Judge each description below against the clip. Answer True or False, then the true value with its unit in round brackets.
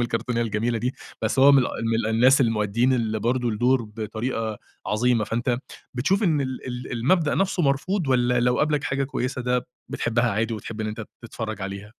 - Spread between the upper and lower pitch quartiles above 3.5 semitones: False (2.8 semitones)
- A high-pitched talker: False (120 Hz)